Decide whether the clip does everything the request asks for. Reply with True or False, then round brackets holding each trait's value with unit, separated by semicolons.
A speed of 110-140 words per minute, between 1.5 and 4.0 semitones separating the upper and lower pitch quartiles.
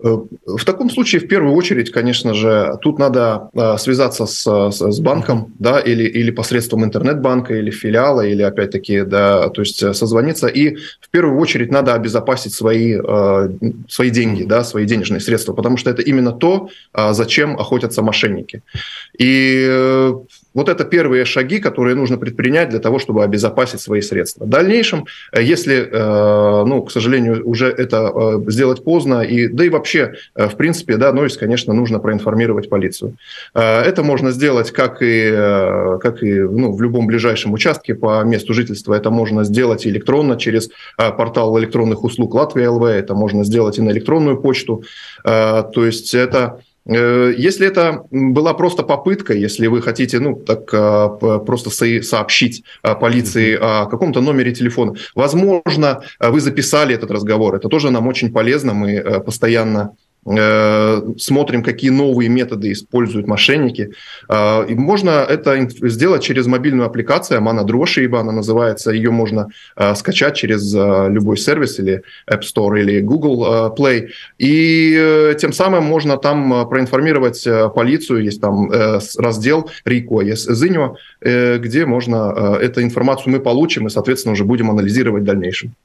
False (150 wpm; 3.3 semitones)